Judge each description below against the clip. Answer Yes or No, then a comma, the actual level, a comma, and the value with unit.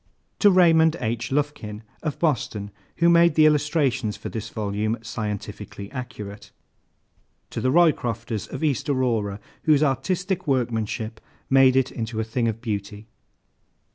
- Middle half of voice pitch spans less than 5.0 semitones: No, wide, 5.5 semitones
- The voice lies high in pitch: No, low, 125 Hz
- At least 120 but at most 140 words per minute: Yes, slow, 135 wpm